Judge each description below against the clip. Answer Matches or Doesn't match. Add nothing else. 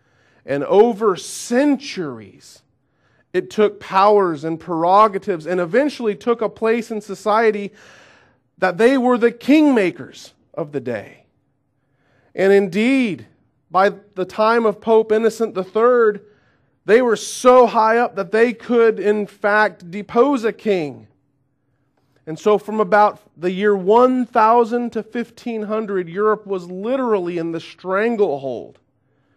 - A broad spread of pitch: Matches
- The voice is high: Matches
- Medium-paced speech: Doesn't match